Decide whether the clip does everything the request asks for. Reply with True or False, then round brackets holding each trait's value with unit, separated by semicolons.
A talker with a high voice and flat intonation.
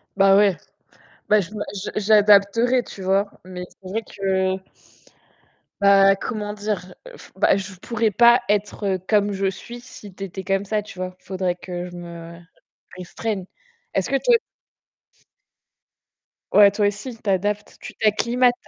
True (200 Hz; 2.1 semitones)